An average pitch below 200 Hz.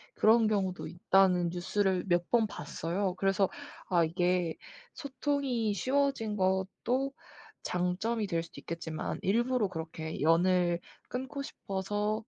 Yes: high, 190 Hz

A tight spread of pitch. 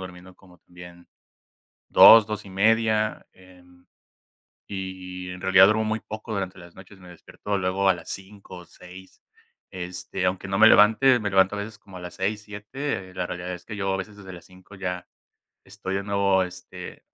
Yes: narrow, 2.2 semitones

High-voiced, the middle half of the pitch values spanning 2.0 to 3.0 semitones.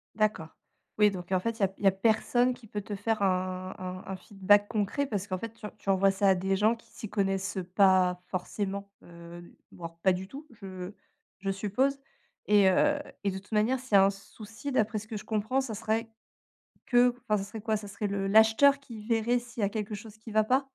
Yes: high, 205 Hz; average, 2.7 semitones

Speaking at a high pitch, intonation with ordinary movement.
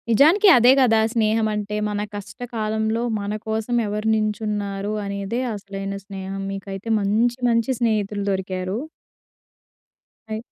No: high, 210 Hz; narrow, 2.1 semitones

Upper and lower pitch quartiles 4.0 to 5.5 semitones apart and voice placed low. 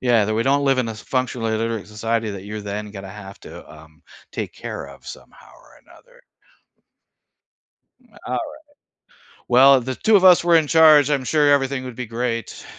Yes: average, 4.7 semitones; low, 120 Hz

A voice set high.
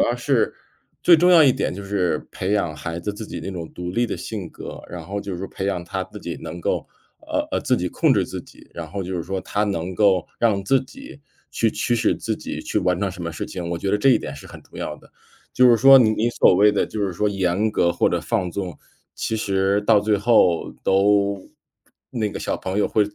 No: low, 100 Hz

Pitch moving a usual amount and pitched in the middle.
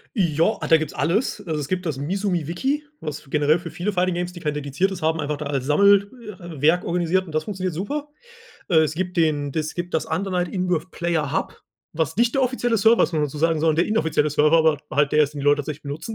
Yes: average, 3.6 semitones; medium, 165 Hz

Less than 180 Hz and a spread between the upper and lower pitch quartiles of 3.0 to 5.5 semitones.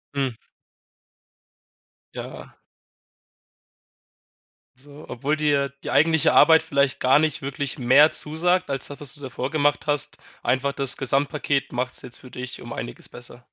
No: medium, 140 Hz; narrow, 2.4 semitones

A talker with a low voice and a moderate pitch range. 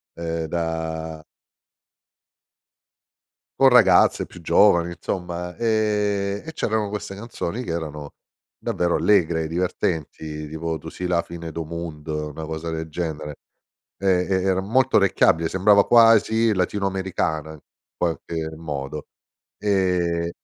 Yes: very low, 85 Hz; average, 3.5 semitones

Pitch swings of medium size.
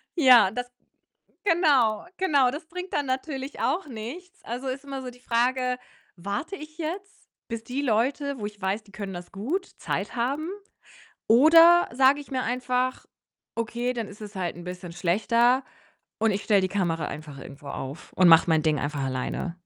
No: wide, 6.2 semitones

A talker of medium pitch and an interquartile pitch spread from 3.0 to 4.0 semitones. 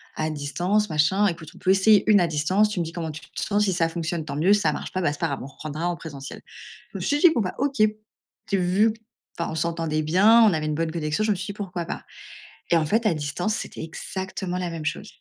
No: medium, 175 Hz; average, 4.4 semitones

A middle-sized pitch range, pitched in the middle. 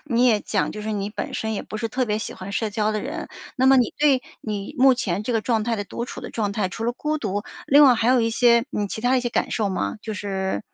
No: average, 3.0 semitones; high, 225 Hz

